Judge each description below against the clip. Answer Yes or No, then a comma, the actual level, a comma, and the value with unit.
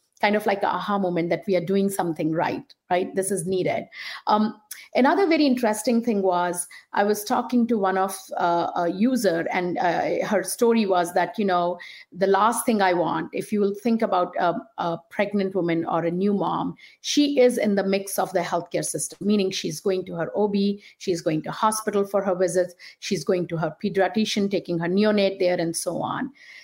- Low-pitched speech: No, high, 190 Hz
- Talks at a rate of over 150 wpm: Yes, fast, 205 wpm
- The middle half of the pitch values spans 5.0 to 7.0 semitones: No, average, 3.0 semitones